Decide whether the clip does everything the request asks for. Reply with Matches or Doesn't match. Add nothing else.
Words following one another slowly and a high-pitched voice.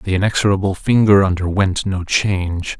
Doesn't match